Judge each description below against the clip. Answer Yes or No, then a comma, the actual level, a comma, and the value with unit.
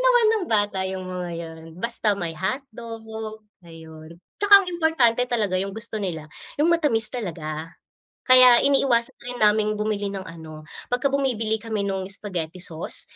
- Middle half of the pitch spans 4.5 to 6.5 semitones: Yes, wide, 5.5 semitones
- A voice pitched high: Yes, high, 215 Hz